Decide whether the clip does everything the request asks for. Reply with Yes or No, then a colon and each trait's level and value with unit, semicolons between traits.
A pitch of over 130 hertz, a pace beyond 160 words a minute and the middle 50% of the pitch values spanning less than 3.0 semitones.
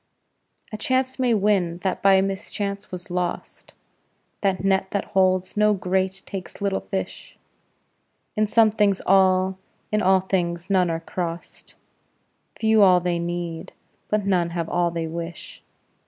No: high, 190 Hz; average, 140 wpm; narrow, 2.4 semitones